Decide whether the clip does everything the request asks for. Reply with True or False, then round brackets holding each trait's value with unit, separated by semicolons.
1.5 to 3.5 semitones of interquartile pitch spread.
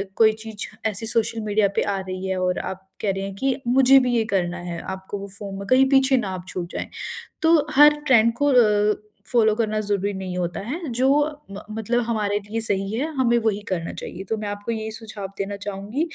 True (3.2 semitones)